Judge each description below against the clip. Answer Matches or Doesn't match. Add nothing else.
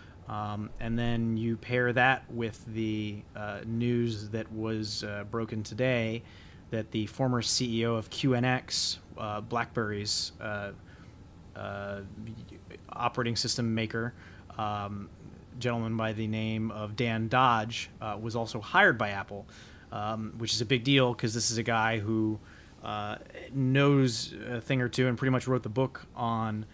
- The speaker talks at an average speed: Matches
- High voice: Doesn't match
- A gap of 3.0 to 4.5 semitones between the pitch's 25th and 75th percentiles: Doesn't match